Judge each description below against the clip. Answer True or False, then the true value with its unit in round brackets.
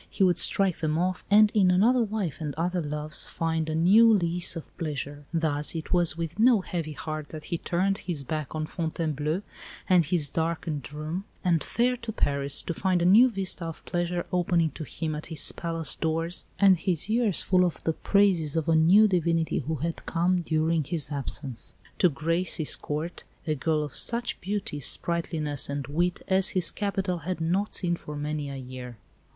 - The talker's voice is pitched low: False (165 Hz)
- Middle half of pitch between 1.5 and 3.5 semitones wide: True (3.2 semitones)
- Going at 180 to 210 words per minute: True (190 wpm)